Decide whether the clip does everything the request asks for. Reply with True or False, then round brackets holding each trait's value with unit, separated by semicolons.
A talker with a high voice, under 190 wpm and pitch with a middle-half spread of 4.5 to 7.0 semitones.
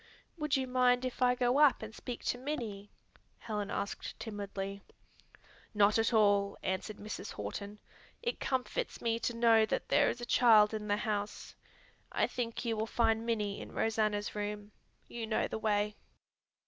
False (220 Hz; 165 wpm; 2.8 semitones)